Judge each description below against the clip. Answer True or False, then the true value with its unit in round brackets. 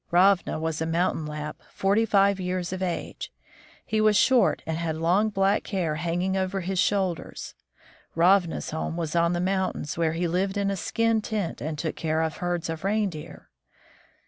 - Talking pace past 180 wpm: False (175 wpm)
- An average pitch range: True (3.3 semitones)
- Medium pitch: True (180 Hz)